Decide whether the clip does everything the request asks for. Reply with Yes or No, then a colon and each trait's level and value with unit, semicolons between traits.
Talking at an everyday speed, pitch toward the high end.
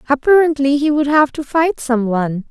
Yes: average, 170 wpm; very high, 280 Hz